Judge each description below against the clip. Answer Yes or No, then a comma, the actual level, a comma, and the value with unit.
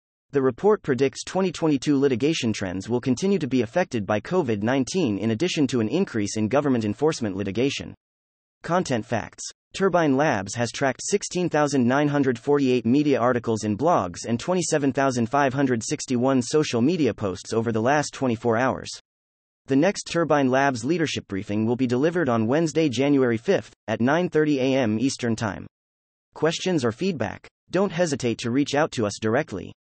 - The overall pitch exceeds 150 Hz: No, low, 130 Hz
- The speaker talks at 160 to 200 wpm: No, average, 145 wpm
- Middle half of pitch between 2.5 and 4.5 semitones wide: No, wide, 5.4 semitones